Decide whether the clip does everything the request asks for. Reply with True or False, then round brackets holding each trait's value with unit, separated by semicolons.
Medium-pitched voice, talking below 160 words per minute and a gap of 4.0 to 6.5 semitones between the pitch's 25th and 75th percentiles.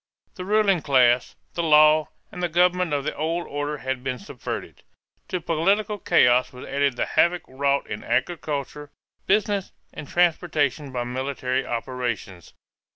True (145 Hz; 145 wpm; 5.4 semitones)